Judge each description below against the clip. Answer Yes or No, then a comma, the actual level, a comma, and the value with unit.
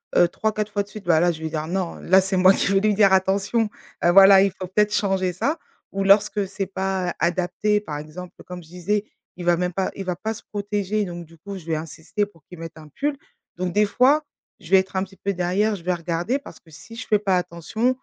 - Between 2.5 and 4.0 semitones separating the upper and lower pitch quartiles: Yes, average, 2.9 semitones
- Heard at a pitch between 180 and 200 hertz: Yes, high, 190 Hz